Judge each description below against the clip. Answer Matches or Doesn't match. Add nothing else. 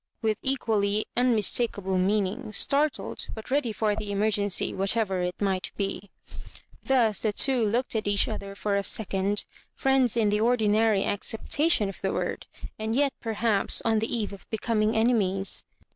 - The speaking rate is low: Doesn't match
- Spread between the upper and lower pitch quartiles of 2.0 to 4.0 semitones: Matches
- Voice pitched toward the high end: Matches